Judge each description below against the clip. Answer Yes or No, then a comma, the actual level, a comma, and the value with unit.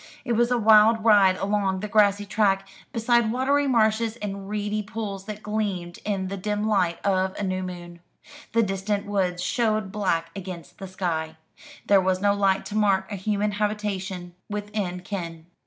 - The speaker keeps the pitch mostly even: Yes, narrow, 2.2 semitones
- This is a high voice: Yes, high, 200 Hz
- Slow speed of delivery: No, average, 170 wpm